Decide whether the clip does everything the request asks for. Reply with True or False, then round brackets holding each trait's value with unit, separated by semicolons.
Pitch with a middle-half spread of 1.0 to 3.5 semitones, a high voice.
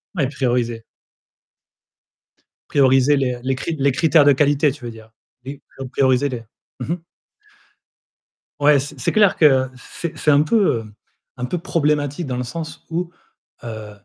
False (3.2 semitones; 140 Hz)